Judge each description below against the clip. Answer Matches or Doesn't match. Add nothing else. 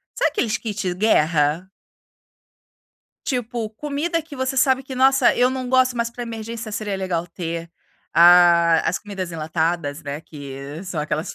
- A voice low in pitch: Doesn't match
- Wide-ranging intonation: Matches